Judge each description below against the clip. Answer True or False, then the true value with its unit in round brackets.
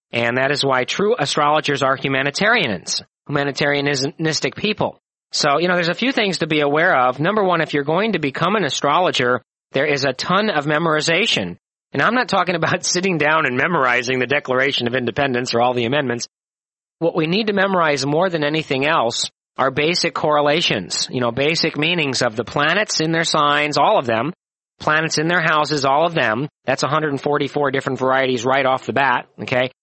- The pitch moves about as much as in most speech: True (3.8 semitones)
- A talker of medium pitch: True (145 Hz)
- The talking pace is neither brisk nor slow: True (190 wpm)